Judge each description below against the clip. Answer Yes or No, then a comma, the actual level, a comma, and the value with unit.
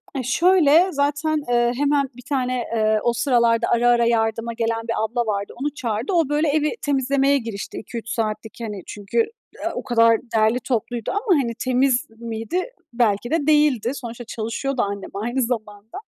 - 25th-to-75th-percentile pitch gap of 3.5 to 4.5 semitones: Yes, average, 3.9 semitones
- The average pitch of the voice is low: No, high, 240 Hz